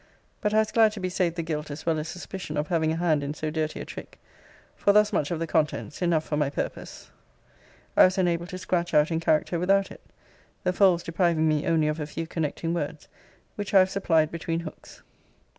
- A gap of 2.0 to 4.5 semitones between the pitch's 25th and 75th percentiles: Yes, average, 2.9 semitones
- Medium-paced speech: No, fast, 225 wpm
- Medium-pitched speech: Yes, medium, 165 Hz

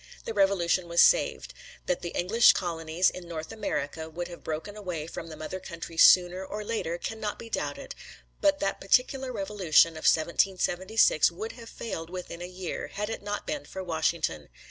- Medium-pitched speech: Yes, medium, 180 Hz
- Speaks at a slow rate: No, average, 175 wpm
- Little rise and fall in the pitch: No, average, 3.8 semitones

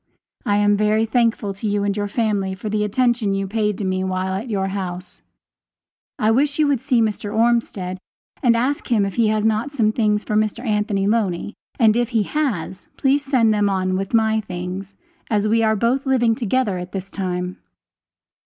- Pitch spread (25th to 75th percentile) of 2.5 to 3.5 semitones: Yes, average, 3.0 semitones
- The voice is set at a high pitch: Yes, high, 215 Hz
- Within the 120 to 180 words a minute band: No, average, 195 wpm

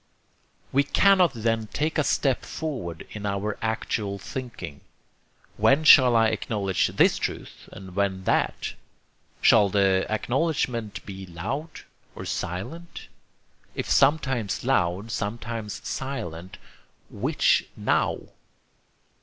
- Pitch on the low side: Yes, low, 110 Hz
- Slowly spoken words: Yes, slow, 105 wpm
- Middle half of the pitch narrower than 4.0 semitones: No, wide, 5.6 semitones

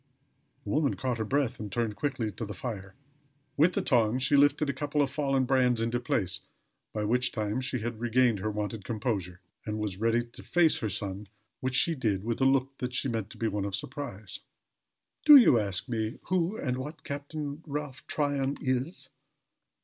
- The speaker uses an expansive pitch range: No, average, 4.5 semitones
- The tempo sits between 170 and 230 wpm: Yes, average, 195 wpm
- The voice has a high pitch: No, low, 125 Hz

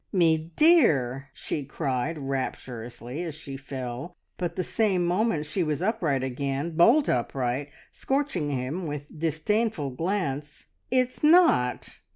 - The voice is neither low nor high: Yes, medium, 155 Hz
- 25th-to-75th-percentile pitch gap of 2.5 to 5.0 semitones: No, wide, 5.5 semitones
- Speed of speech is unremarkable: No, slow, 125 wpm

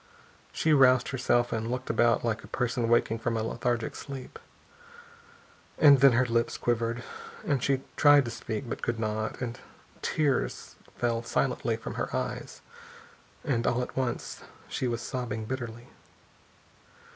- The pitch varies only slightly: Yes, narrow, 2.1 semitones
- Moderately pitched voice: No, low, 120 Hz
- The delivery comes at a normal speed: Yes, average, 145 wpm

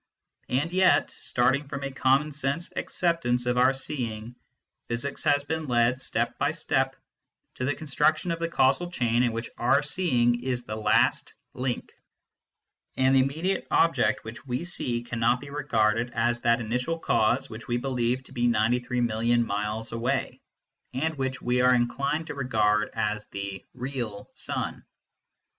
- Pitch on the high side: No, low, 125 Hz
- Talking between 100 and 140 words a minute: No, average, 165 wpm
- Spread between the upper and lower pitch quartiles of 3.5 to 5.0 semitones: No, average, 3.0 semitones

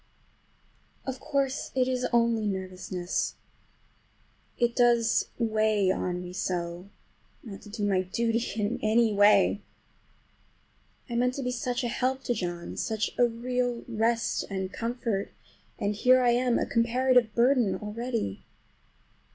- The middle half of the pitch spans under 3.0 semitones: No, average, 3.4 semitones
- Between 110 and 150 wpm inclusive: Yes, slow, 135 wpm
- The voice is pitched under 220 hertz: No, high, 230 Hz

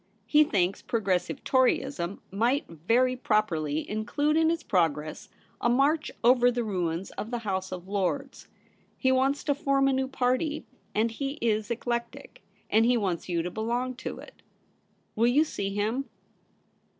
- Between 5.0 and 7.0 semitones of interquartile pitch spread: Yes, wide, 5.4 semitones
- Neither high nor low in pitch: No, high, 235 Hz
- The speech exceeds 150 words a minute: Yes, average, 160 wpm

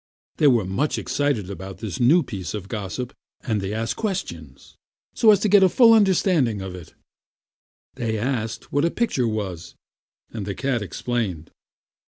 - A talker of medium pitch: No, low, 115 Hz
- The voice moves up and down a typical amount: No, wide, 7.0 semitones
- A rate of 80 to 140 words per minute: No, average, 170 wpm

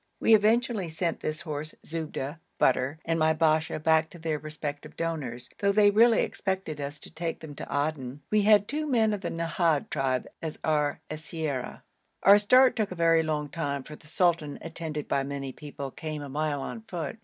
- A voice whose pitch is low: No, medium, 160 Hz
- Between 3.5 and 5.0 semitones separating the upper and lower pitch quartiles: Yes, average, 3.8 semitones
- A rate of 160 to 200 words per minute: Yes, average, 190 wpm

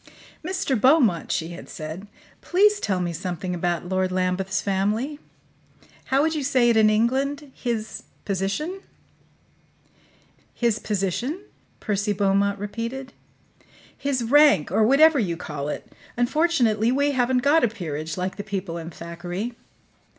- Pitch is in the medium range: No, high, 215 Hz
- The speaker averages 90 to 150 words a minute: Yes, slow, 135 wpm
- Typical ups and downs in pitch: No, wide, 6.5 semitones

